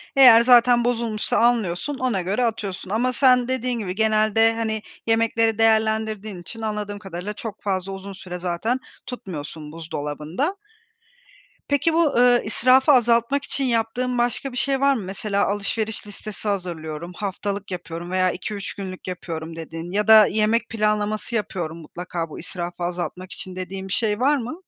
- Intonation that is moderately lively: Yes, average, 4.3 semitones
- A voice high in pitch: Yes, high, 215 Hz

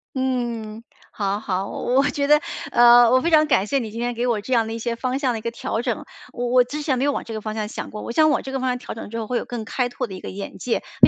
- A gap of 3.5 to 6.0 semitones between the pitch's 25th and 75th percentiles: No, average, 2.7 semitones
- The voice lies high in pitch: Yes, high, 240 Hz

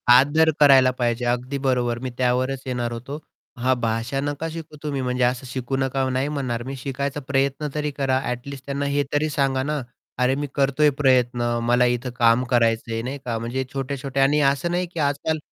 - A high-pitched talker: No, low, 135 Hz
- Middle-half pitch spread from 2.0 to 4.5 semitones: Yes, narrow, 2.4 semitones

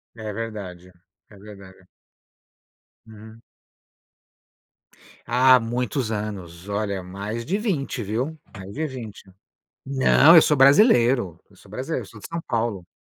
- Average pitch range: Yes, average, 4.7 semitones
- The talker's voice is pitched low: Yes, low, 110 Hz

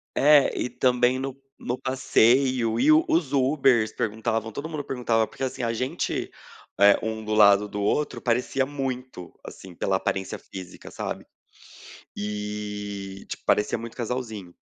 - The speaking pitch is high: No, low, 115 Hz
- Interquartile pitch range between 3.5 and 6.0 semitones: Yes, average, 3.9 semitones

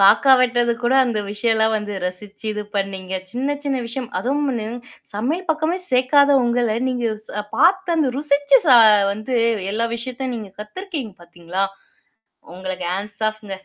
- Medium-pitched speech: No, high, 235 Hz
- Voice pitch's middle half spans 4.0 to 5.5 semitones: Yes, average, 4.8 semitones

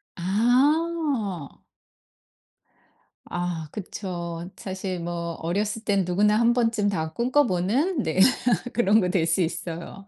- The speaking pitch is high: Yes, high, 195 Hz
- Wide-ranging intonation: No, average, 5.0 semitones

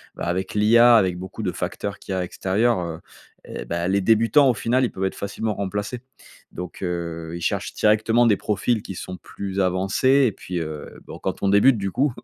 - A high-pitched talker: No, low, 100 Hz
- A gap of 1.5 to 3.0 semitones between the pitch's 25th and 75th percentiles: No, average, 3.8 semitones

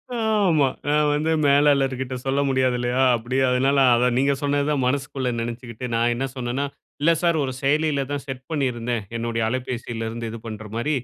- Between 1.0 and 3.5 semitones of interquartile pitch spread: Yes, average, 3.0 semitones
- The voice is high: No, low, 130 Hz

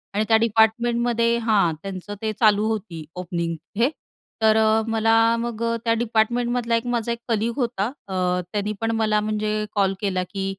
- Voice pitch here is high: Yes, high, 220 Hz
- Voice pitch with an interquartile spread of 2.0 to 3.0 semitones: Yes, narrow, 2.4 semitones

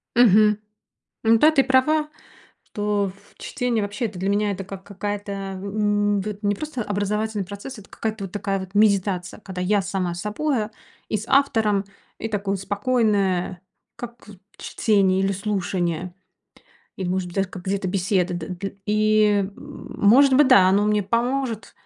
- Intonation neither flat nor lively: No, narrow, 2.1 semitones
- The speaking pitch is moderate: No, high, 205 Hz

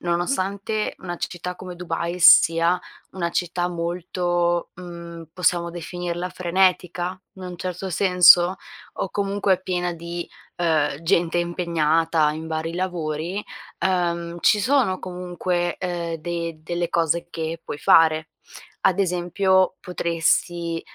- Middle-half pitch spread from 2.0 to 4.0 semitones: No, narrow, 1.4 semitones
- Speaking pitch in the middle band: Yes, medium, 175 Hz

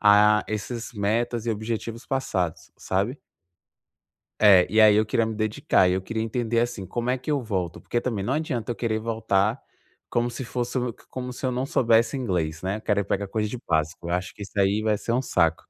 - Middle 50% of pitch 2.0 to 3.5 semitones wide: Yes, average, 3.2 semitones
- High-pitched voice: No, low, 110 Hz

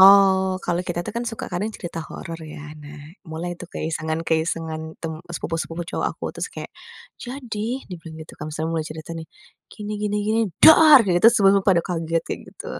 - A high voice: No, medium, 175 Hz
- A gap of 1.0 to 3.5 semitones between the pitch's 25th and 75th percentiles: No, average, 4.0 semitones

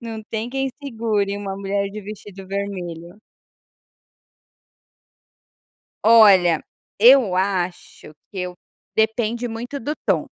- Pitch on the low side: No, high, 205 Hz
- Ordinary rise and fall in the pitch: Yes, average, 3.0 semitones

